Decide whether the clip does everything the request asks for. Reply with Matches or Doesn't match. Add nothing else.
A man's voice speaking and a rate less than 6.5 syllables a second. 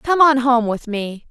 Doesn't match